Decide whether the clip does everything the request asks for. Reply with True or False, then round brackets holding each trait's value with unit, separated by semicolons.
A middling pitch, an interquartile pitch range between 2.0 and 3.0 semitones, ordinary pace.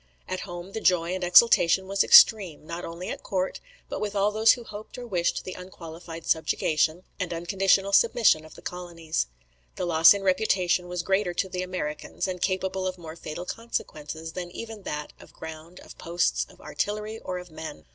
True (180 Hz; 2.7 semitones; 185 wpm)